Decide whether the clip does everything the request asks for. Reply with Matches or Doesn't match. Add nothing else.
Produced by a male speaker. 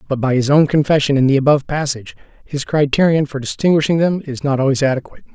Matches